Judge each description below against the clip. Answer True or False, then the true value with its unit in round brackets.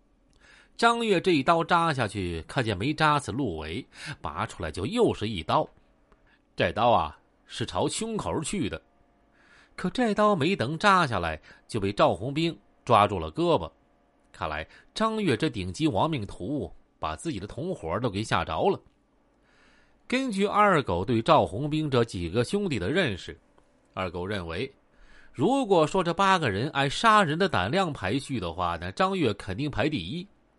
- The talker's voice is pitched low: False (150 Hz)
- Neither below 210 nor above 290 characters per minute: True (230 characters per minute)